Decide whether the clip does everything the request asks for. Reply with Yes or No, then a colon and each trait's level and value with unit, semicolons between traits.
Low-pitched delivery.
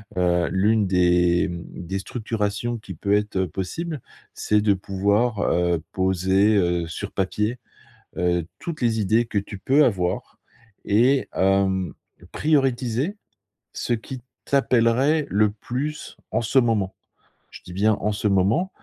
Yes: low, 105 Hz